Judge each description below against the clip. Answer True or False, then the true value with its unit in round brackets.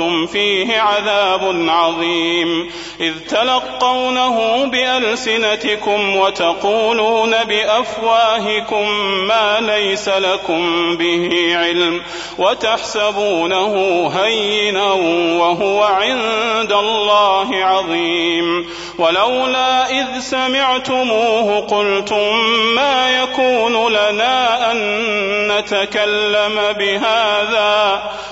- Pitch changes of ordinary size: True (3.0 semitones)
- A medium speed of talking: False (60 wpm)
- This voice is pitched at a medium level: False (210 Hz)